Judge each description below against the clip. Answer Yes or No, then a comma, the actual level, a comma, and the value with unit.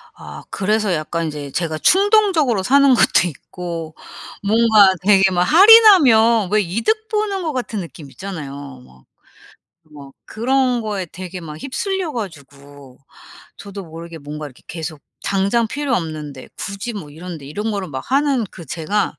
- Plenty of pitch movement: Yes, wide, 7.5 semitones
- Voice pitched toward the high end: Yes, high, 195 Hz